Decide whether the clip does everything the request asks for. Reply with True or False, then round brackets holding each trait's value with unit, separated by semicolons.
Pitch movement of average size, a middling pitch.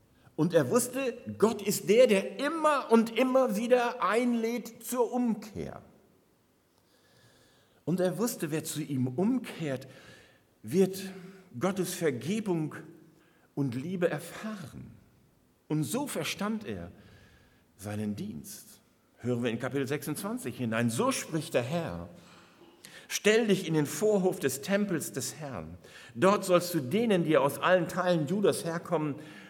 False (7.3 semitones; 175 Hz)